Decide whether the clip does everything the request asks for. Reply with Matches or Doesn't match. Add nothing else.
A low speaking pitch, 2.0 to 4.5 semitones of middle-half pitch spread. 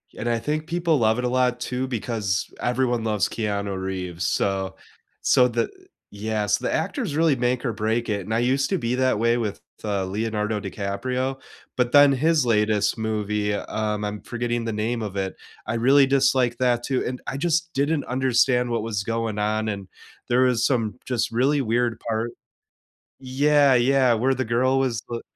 Matches